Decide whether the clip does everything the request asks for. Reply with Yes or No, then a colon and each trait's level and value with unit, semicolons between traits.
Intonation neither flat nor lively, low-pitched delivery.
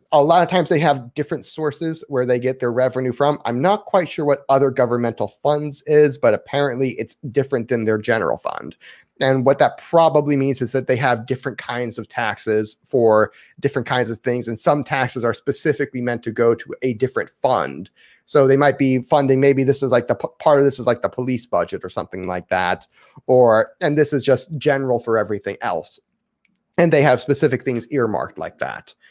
Yes: average, 3.3 semitones; low, 130 Hz